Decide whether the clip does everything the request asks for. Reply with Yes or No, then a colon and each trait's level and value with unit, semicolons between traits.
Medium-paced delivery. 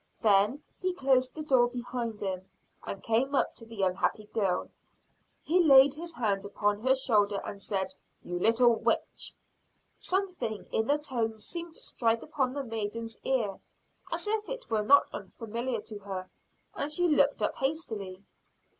Yes: average, 160 wpm